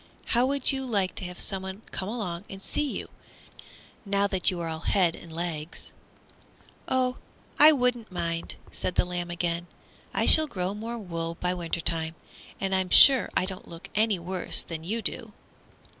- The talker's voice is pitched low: No, medium, 185 Hz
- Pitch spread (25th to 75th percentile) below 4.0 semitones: No, average, 4.6 semitones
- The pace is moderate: Yes, average, 175 wpm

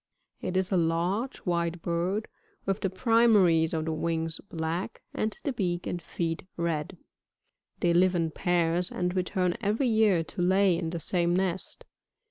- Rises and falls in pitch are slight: Yes, narrow, 2.3 semitones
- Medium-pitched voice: Yes, medium, 175 Hz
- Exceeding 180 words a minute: No, average, 160 wpm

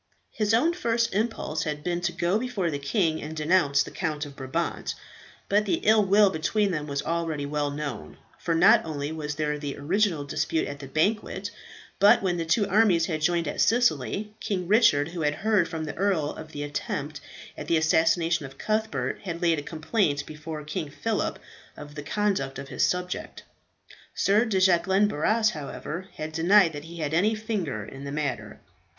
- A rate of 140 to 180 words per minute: No, average, 190 wpm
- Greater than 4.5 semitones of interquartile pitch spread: Yes, average, 5.2 semitones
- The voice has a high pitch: No, medium, 165 Hz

